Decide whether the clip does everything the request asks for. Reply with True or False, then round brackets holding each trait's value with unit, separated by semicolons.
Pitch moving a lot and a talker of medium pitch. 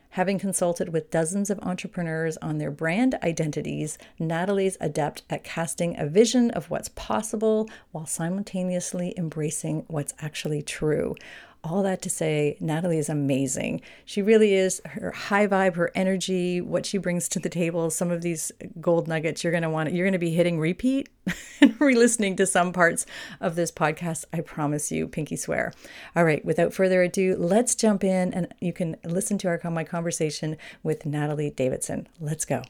False (3.3 semitones; 175 Hz)